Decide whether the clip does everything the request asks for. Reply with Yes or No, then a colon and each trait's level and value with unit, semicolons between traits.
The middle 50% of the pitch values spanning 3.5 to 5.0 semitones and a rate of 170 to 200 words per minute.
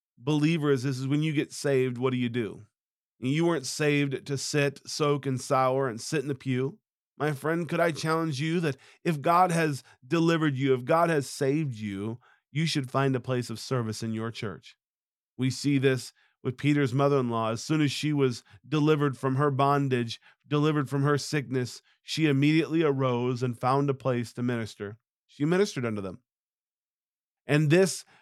No: average, 3.0 semitones; average, 185 wpm